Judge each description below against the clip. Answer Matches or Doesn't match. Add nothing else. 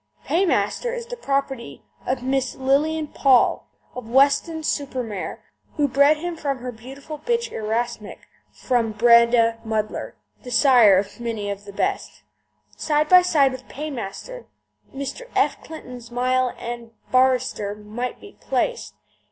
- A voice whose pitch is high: Matches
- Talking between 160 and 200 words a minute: Doesn't match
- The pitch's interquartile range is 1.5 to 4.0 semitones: Doesn't match